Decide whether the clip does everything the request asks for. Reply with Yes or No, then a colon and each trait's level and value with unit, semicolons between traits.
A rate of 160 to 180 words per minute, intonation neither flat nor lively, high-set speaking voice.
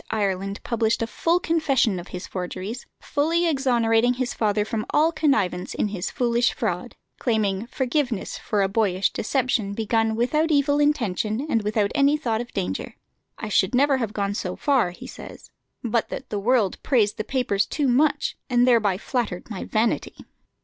Yes: average, 170 wpm; average, 4.5 semitones; high, 230 Hz